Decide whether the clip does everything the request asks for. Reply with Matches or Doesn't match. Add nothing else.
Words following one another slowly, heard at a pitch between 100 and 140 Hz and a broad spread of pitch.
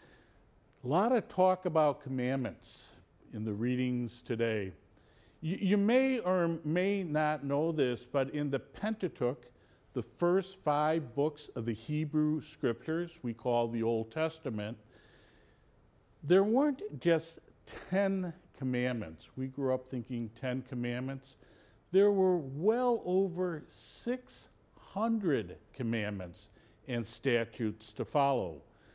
Matches